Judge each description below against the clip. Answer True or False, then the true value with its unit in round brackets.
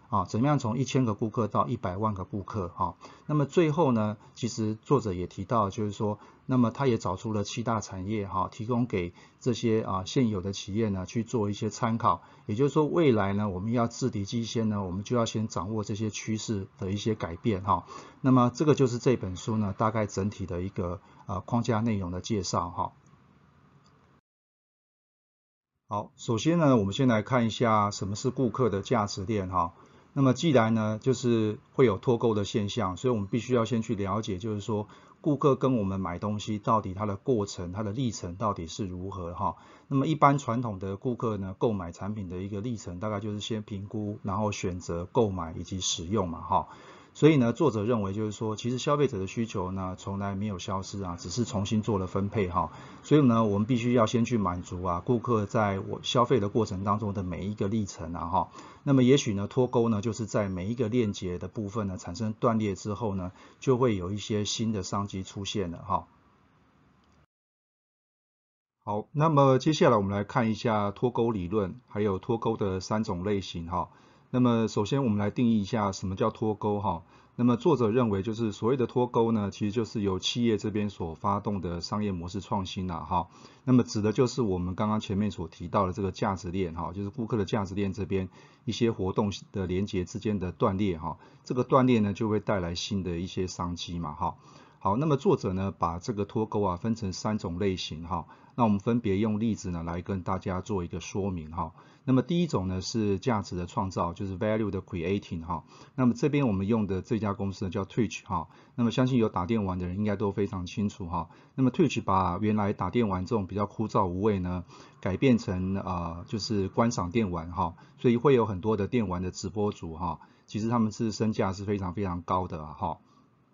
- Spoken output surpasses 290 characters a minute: True (320 characters per minute)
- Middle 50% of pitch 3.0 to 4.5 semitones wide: True (3.6 semitones)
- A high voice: False (105 Hz)